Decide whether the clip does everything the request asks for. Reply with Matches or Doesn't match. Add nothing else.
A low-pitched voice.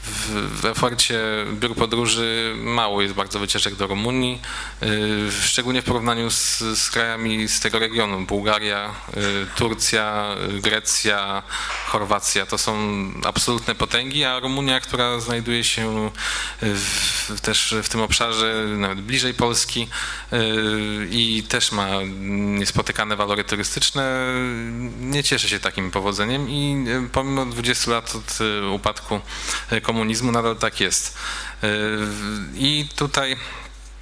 Matches